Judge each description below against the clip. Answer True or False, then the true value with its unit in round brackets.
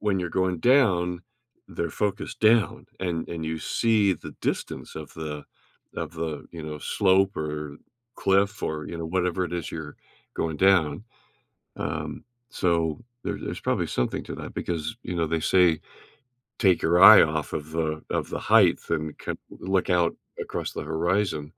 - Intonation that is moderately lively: True (3.3 semitones)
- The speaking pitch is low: True (85 Hz)